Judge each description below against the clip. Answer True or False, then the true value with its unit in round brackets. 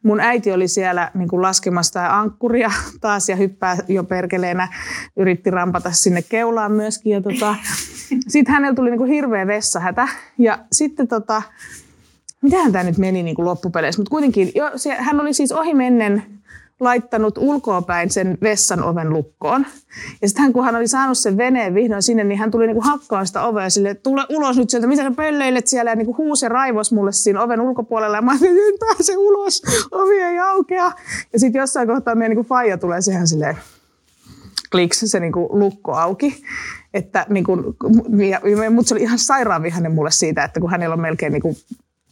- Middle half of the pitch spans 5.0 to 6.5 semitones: True (5.4 semitones)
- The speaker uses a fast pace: True (185 wpm)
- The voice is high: True (220 Hz)